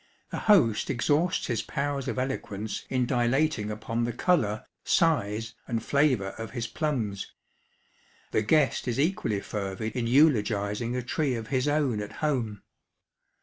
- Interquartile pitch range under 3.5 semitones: No, average, 4.8 semitones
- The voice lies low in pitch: Yes, low, 120 Hz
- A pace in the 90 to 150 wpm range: Yes, average, 145 wpm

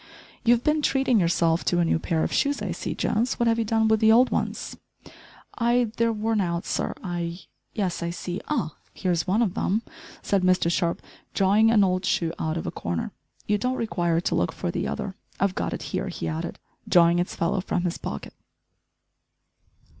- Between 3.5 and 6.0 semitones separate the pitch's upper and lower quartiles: Yes, average, 4.7 semitones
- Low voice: No, medium, 185 Hz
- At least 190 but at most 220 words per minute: Yes, fast, 205 wpm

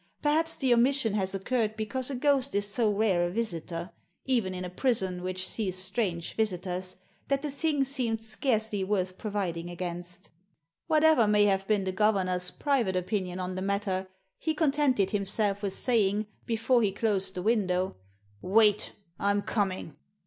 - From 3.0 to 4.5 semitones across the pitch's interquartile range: Yes, average, 4.1 semitones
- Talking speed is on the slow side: No, average, 165 wpm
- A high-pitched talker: Yes, high, 205 Hz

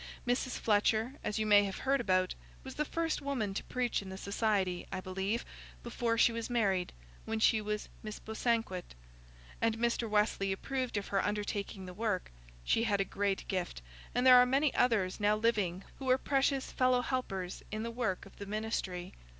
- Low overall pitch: No, high, 215 Hz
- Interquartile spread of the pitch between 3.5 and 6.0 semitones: Yes, average, 3.8 semitones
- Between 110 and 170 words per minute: No, average, 185 wpm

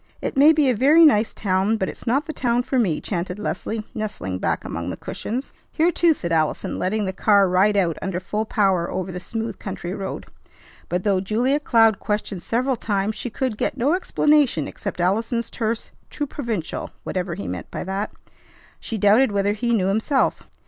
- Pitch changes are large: No, average, 4.6 semitones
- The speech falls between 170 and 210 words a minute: Yes, average, 190 wpm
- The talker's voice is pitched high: Yes, high, 215 Hz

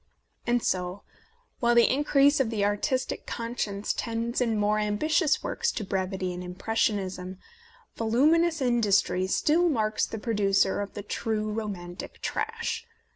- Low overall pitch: No, high, 220 Hz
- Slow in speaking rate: Yes, slow, 130 wpm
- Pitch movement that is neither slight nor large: Yes, average, 4.4 semitones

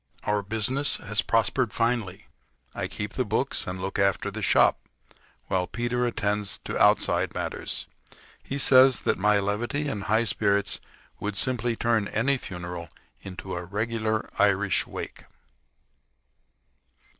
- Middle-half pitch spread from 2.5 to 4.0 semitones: Yes, average, 3.2 semitones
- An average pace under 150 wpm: Yes, slow, 135 wpm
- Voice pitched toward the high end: No, low, 105 Hz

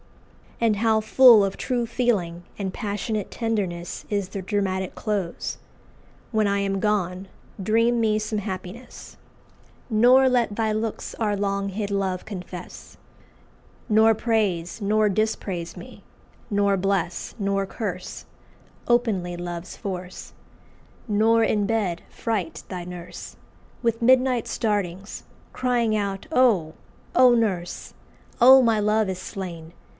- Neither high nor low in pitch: No, high, 205 Hz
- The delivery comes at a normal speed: No, slow, 120 wpm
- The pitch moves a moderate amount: Yes, average, 3.2 semitones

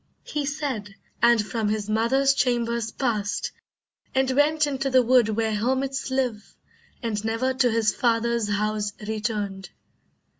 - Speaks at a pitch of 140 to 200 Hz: No, high, 235 Hz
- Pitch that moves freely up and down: No, average, 3.6 semitones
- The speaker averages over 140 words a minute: No, slow, 135 wpm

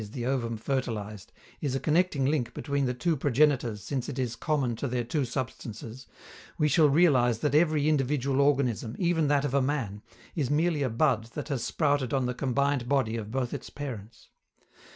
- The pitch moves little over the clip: No, average, 3.4 semitones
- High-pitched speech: No, low, 135 Hz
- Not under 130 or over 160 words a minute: No, average, 190 wpm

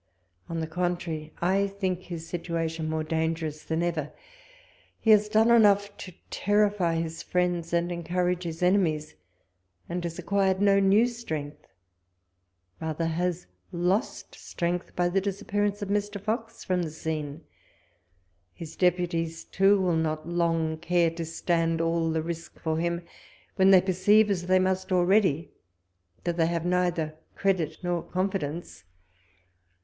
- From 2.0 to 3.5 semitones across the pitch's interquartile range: Yes, average, 2.8 semitones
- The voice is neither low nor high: Yes, medium, 175 Hz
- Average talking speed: Yes, average, 145 wpm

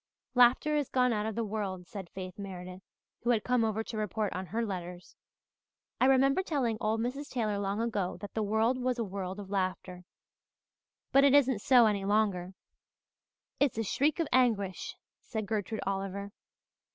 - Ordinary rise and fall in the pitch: Yes, average, 4.0 semitones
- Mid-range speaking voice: No, high, 215 Hz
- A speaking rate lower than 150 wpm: No, average, 175 wpm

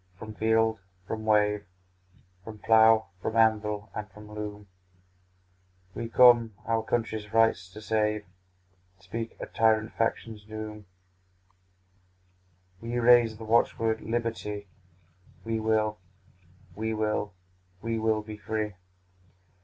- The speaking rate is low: Yes, slow, 115 wpm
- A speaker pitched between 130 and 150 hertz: No, low, 110 Hz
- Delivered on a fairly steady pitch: Yes, narrow, 1.0 semitones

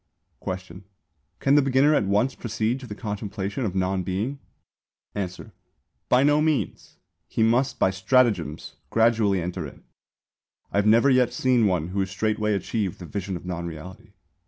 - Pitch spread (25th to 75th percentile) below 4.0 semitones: No, average, 4.7 semitones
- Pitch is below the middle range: Yes, low, 105 Hz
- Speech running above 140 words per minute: Yes, average, 155 wpm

